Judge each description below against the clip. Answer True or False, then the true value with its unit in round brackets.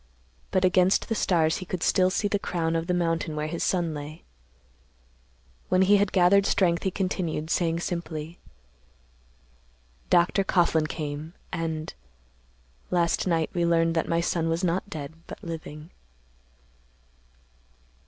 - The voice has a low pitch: False (170 Hz)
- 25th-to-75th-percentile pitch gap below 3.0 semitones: True (2.5 semitones)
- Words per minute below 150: True (135 wpm)